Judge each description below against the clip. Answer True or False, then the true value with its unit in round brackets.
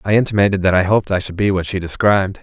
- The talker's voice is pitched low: True (95 Hz)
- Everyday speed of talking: False (270 wpm)